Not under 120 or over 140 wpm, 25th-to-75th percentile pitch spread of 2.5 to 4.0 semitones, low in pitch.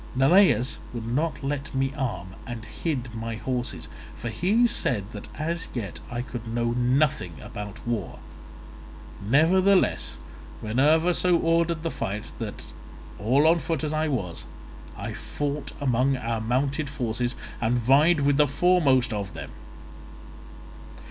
No: slow, 135 wpm; average, 5.1 semitones; low, 130 Hz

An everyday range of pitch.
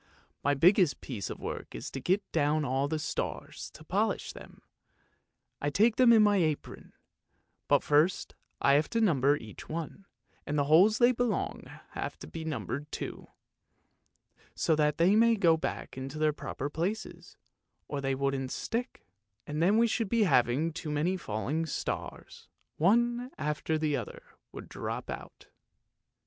No: wide, 5.9 semitones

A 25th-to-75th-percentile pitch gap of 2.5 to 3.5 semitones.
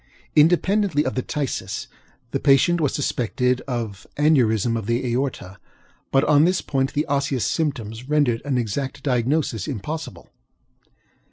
No: average, 3.9 semitones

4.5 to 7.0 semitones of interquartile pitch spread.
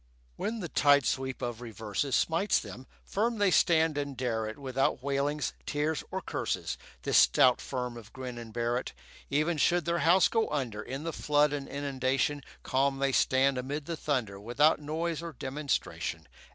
No: average, 3.4 semitones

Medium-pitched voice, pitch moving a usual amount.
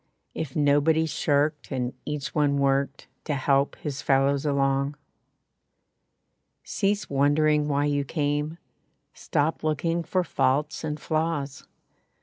No: medium, 145 Hz; narrow, 1.7 semitones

